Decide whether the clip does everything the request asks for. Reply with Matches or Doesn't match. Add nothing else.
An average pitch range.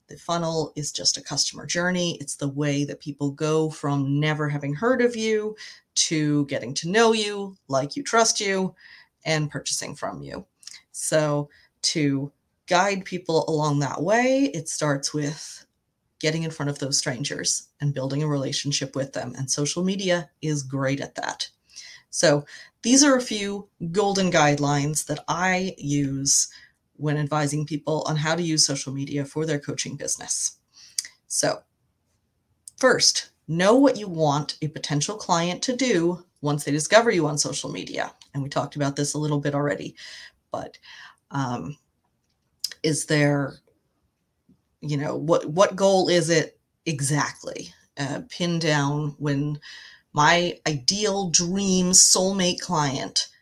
Matches